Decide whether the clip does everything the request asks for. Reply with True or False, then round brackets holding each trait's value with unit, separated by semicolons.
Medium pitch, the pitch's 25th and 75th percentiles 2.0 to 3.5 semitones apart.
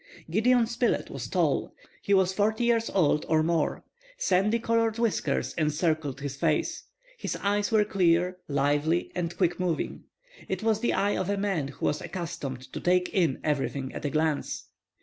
False (180 Hz; 5.2 semitones)